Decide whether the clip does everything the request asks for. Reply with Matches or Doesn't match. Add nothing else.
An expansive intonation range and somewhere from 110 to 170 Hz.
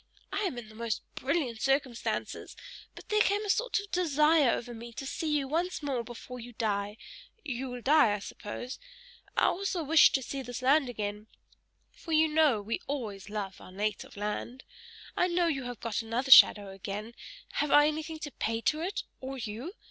Doesn't match